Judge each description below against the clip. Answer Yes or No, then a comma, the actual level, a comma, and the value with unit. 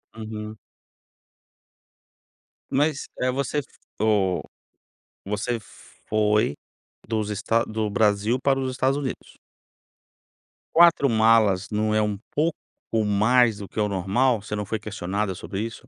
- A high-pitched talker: No, low, 110 Hz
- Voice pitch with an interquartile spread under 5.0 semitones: Yes, average, 3.3 semitones